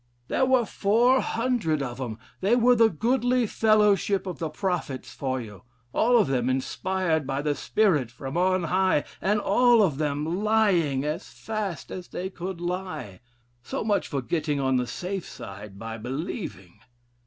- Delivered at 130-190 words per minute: Yes, average, 160 wpm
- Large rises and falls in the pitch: Yes, wide, 7.7 semitones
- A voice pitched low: No, medium, 180 Hz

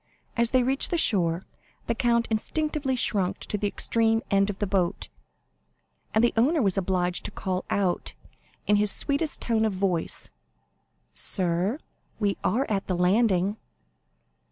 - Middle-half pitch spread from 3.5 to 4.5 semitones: Yes, average, 3.9 semitones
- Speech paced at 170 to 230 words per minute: No, average, 150 wpm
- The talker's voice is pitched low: No, high, 210 Hz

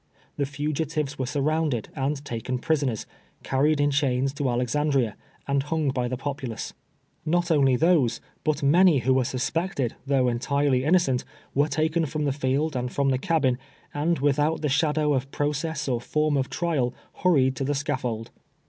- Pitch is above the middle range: No, medium, 140 Hz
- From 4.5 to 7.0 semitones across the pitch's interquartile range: No, average, 2.8 semitones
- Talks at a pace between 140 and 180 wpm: Yes, average, 165 wpm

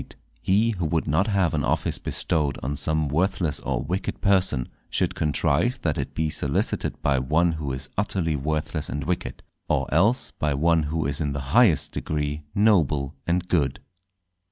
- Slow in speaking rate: No, average, 170 wpm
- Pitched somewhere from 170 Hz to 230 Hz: No, very low, 80 Hz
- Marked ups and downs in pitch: No, average, 3.8 semitones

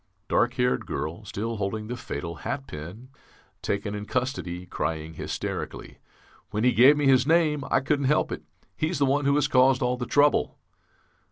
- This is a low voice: Yes, low, 125 Hz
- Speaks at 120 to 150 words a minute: No, average, 175 wpm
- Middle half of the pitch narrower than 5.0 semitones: No, wide, 5.5 semitones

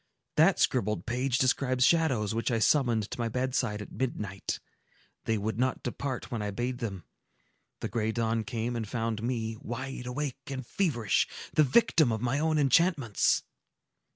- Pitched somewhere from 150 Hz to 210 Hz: No, low, 120 Hz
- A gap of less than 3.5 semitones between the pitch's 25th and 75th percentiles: Yes, average, 2.9 semitones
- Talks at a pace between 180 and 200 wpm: No, average, 160 wpm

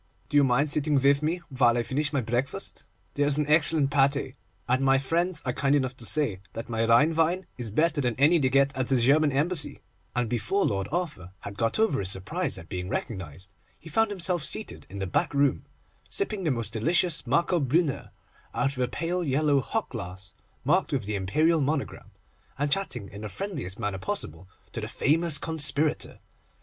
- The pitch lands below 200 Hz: Yes, medium, 140 Hz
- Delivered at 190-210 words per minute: Yes, average, 195 wpm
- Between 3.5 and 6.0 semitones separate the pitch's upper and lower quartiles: Yes, average, 5.1 semitones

